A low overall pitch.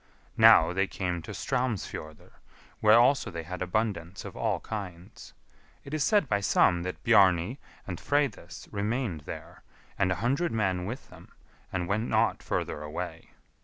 Yes: low, 100 Hz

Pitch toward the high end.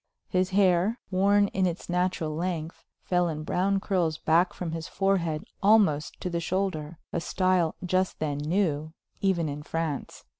No: medium, 175 Hz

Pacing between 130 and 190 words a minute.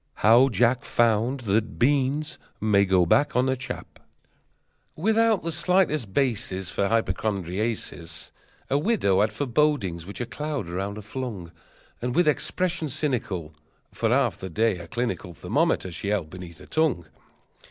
Yes: average, 145 wpm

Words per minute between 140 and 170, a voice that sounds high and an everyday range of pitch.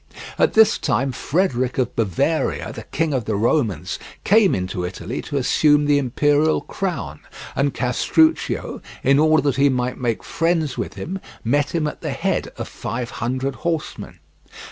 No: average, 160 wpm; medium, 140 Hz; average, 4.4 semitones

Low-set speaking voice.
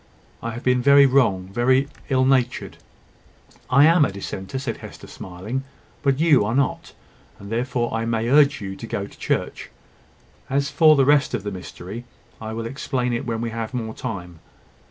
Yes: low, 120 Hz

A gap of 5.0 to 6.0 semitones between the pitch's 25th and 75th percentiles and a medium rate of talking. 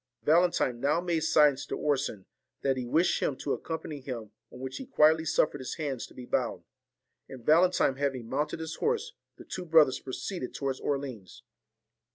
No: average, 3.7 semitones; average, 180 wpm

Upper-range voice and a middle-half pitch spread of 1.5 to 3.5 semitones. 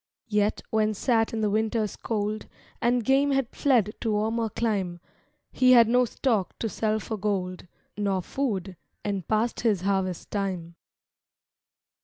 Yes: high, 215 Hz; average, 2.8 semitones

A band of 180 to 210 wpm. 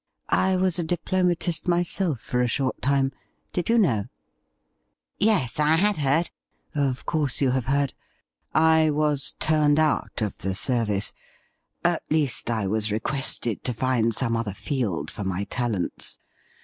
No: average, 160 wpm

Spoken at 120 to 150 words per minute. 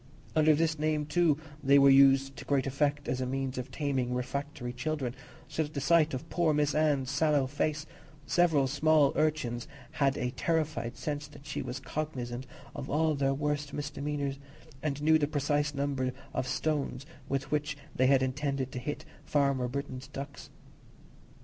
No: average, 170 wpm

